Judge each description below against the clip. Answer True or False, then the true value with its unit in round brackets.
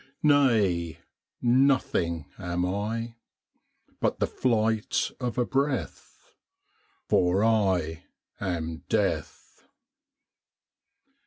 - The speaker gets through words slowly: True (75 wpm)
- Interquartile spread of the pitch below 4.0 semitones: False (5.6 semitones)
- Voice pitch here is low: True (105 Hz)